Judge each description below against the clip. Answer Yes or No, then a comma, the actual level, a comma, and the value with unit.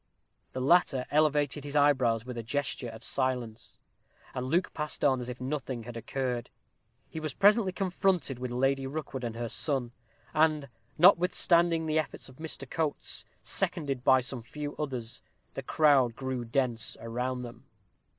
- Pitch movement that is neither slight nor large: Yes, average, 3.7 semitones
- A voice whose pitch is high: No, low, 135 Hz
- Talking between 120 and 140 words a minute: No, average, 155 wpm